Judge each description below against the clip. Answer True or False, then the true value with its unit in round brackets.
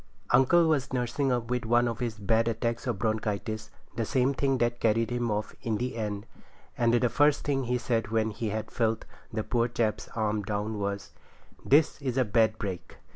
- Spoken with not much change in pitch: True (2.3 semitones)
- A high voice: False (115 Hz)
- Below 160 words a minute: False (190 wpm)